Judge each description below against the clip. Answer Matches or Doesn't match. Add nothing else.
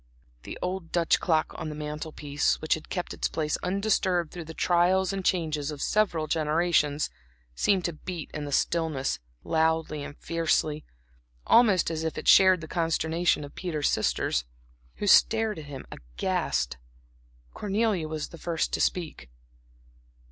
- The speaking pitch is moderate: Matches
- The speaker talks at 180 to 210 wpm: Doesn't match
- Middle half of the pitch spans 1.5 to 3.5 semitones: Matches